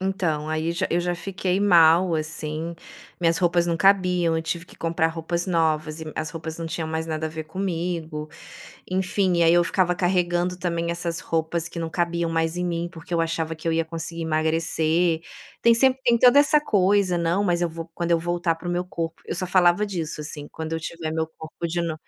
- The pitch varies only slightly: Yes, narrow, 1.7 semitones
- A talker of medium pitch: Yes, medium, 170 Hz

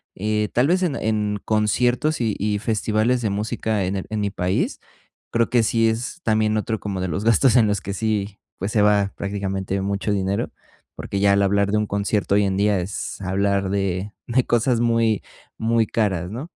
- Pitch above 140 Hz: No, low, 105 Hz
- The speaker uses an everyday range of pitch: No, narrow, 2.2 semitones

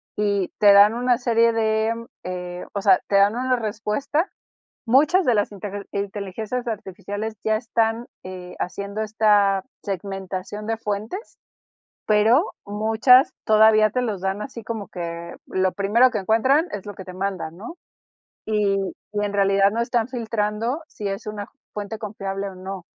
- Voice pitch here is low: No, high, 210 Hz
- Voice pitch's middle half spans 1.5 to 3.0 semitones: Yes, narrow, 2.5 semitones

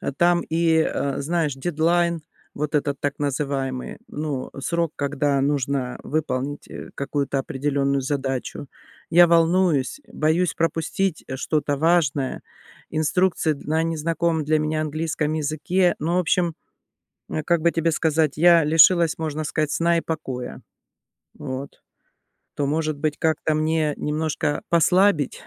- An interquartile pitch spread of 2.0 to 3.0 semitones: Yes, narrow, 2.6 semitones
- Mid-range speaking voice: Yes, medium, 155 Hz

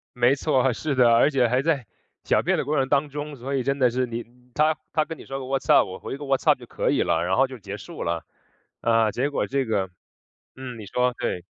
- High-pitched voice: No, low, 130 Hz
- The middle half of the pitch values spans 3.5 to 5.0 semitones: No, average, 3.1 semitones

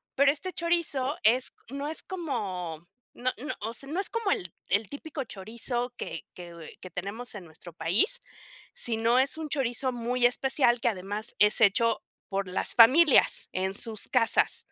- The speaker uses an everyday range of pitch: No, wide, 5.7 semitones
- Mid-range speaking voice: No, high, 240 Hz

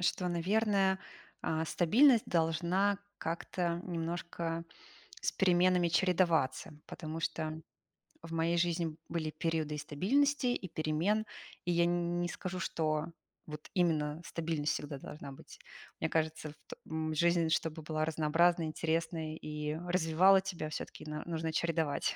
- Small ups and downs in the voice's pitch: Yes, narrow, 2.1 semitones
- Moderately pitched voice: Yes, medium, 165 Hz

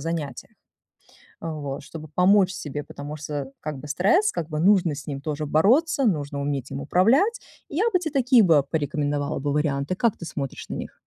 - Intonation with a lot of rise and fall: Yes, wide, 5.7 semitones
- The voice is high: No, medium, 155 Hz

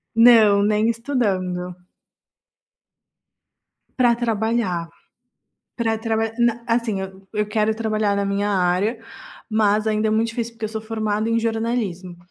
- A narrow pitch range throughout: Yes, narrow, 2.2 semitones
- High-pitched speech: Yes, high, 220 Hz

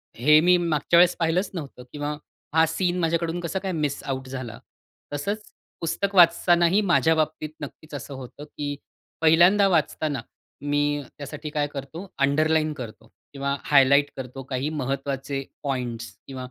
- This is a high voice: No, medium, 150 Hz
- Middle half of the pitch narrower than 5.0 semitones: Yes, average, 3.4 semitones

